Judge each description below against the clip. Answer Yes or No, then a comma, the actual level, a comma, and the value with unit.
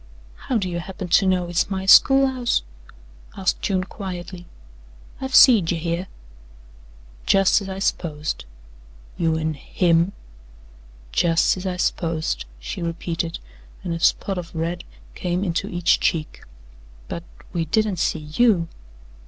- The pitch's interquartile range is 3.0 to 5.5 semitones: No, narrow, 2.5 semitones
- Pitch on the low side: No, medium, 175 Hz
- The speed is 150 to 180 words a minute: No, slow, 135 wpm